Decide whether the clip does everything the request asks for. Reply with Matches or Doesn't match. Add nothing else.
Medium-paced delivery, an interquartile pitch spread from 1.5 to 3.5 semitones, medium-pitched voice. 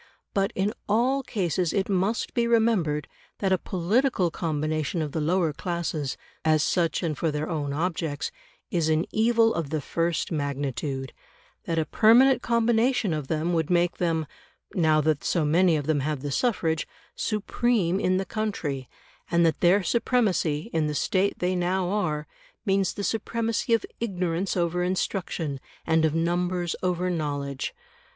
Doesn't match